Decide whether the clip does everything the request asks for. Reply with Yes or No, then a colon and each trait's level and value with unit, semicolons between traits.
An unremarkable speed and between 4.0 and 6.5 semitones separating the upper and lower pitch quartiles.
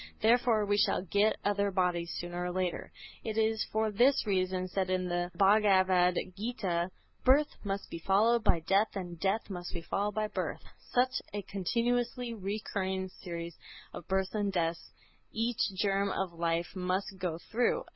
No: average, 160 wpm; average, 3.2 semitones